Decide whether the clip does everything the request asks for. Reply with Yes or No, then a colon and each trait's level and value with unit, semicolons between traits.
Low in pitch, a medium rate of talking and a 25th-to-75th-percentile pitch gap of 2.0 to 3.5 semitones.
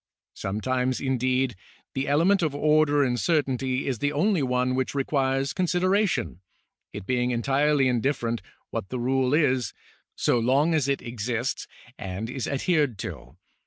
Yes: low, 130 Hz; average, 145 wpm; average, 2.9 semitones